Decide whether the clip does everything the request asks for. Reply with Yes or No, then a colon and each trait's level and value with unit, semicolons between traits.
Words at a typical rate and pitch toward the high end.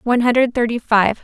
Yes: average, 195 wpm; high, 235 Hz